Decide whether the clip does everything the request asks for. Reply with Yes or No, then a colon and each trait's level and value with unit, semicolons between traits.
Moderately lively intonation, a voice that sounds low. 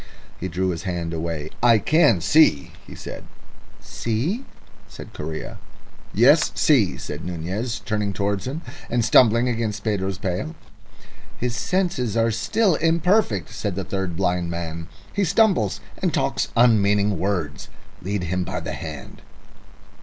No: wide, 5.7 semitones; low, 105 Hz